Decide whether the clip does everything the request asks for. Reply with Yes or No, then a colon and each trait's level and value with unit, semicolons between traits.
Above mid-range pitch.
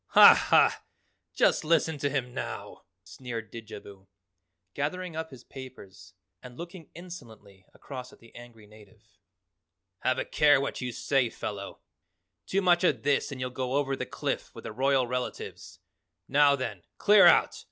No: low, 130 Hz